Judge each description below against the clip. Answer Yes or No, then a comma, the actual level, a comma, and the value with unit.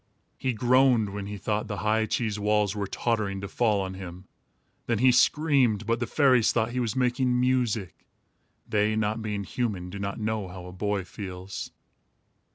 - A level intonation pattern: No, average, 3.3 semitones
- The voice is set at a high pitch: No, low, 110 Hz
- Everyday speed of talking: Yes, average, 175 wpm